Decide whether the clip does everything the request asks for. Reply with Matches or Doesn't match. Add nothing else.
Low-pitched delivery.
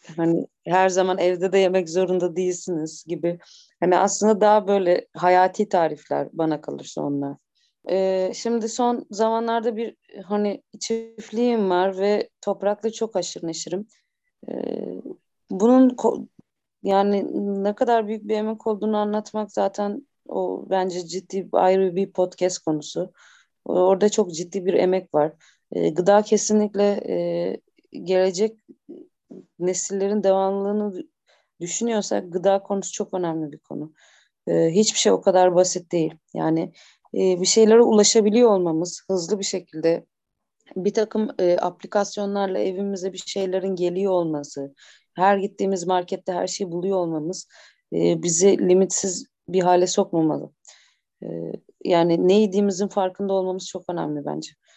Doesn't match